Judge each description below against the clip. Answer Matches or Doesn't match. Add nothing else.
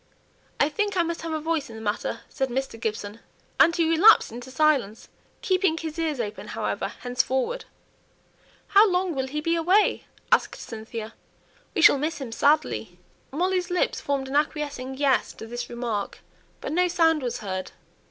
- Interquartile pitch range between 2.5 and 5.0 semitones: Doesn't match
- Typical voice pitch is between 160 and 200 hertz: Doesn't match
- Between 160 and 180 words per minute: Matches